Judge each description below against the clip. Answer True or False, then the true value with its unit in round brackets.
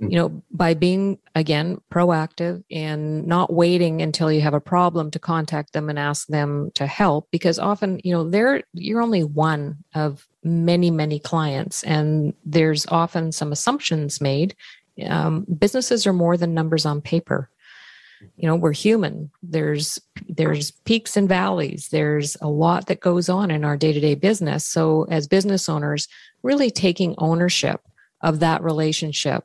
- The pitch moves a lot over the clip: False (2.7 semitones)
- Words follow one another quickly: False (155 wpm)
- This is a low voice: False (165 Hz)